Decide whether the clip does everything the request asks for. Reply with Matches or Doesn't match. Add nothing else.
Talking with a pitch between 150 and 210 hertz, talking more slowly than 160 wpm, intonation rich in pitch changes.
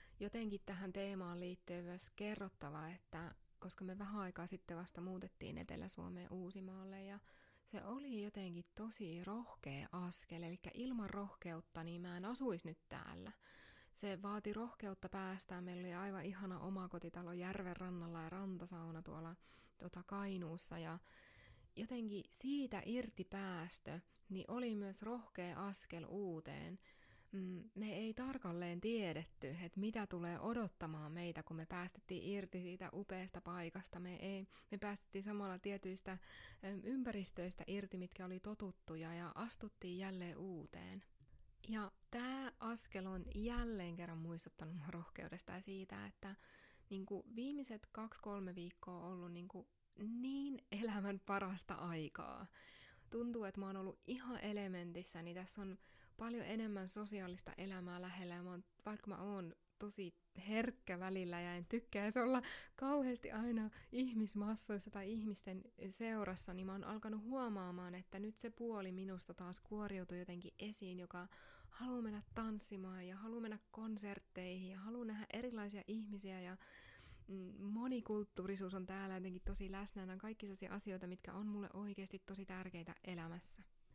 Doesn't match